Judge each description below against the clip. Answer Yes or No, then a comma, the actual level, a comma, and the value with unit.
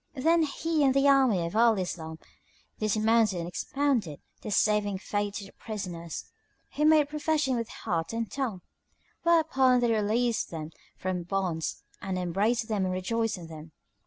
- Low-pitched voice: No, high, 215 Hz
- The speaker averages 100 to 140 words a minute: No, average, 160 wpm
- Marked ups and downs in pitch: Yes, wide, 6.1 semitones